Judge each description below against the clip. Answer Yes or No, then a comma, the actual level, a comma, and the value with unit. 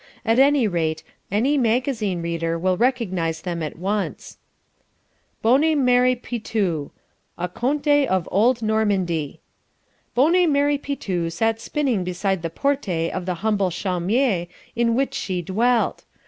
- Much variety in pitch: Yes, wide, 6.2 semitones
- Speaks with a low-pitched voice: No, high, 215 Hz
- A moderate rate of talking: No, slow, 130 wpm